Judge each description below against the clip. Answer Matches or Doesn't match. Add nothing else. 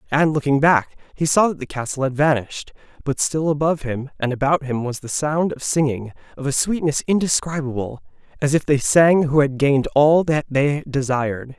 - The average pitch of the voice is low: Doesn't match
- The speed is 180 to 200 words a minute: Matches